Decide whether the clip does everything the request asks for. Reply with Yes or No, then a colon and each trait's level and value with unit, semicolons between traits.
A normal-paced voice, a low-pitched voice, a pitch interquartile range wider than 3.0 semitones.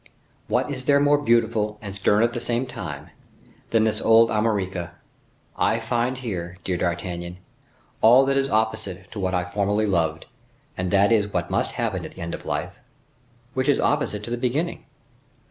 Yes: average, 180 wpm; low, 110 Hz; average, 4.3 semitones